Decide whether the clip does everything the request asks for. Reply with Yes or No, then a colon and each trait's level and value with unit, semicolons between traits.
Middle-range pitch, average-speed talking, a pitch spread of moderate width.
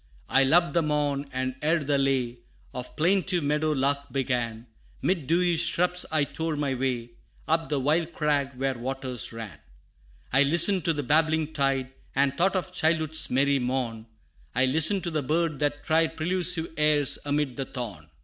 Yes: medium, 145 Hz; average, 170 wpm; average, 3.5 semitones